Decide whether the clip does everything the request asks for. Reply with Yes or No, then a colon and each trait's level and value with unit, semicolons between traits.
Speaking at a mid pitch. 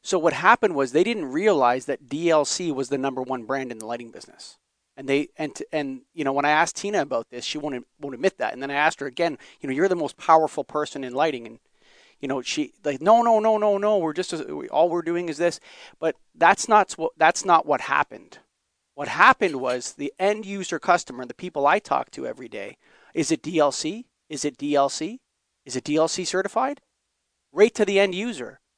Yes: medium, 155 Hz